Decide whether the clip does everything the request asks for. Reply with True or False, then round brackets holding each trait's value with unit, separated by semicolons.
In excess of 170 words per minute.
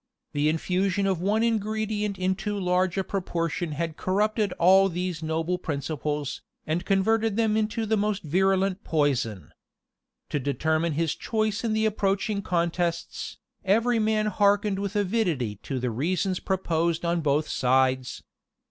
False (140 wpm)